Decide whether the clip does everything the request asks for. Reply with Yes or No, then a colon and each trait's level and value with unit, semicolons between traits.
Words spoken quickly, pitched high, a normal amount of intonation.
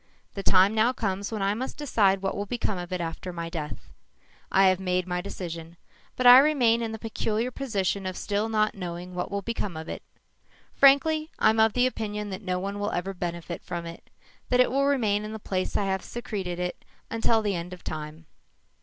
Yes: fast, 210 wpm; high, 200 Hz; average, 3.8 semitones